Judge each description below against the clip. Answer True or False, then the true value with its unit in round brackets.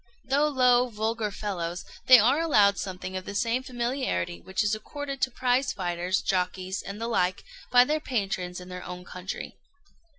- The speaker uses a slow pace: False (170 wpm)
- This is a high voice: True (210 Hz)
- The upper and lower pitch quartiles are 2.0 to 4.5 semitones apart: False (5.5 semitones)